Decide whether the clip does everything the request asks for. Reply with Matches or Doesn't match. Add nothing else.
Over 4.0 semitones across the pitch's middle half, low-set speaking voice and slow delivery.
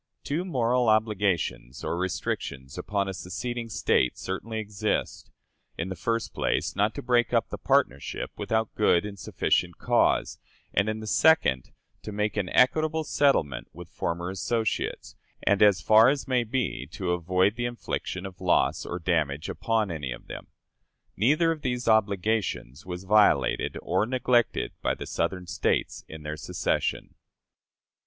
Doesn't match